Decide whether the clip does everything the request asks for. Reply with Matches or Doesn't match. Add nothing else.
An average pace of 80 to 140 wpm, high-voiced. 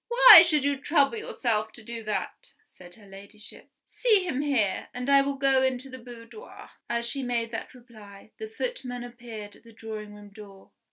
Doesn't match